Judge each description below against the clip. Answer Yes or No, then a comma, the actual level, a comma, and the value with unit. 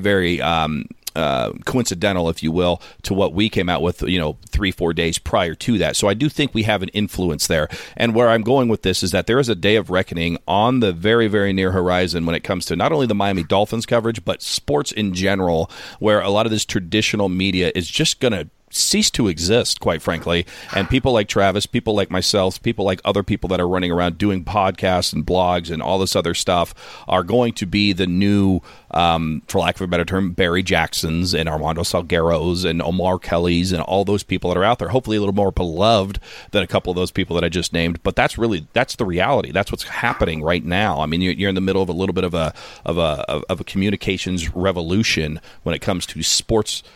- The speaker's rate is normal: No, fast, 235 wpm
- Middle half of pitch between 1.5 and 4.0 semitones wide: Yes, average, 2.9 semitones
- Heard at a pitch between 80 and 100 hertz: Yes, very low, 95 Hz